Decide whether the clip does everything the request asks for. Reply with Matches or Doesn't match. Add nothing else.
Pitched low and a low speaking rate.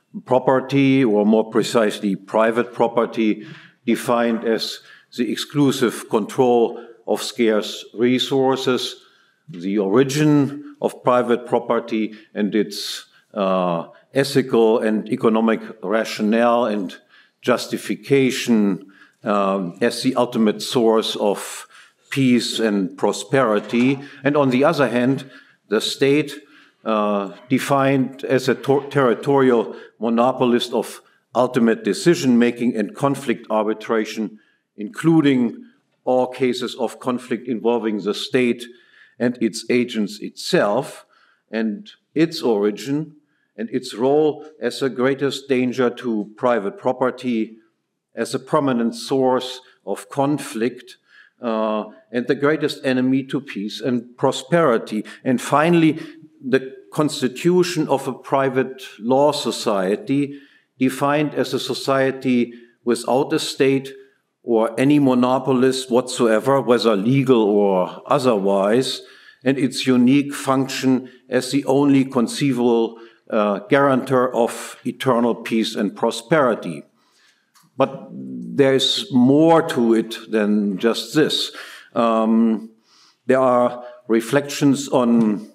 Matches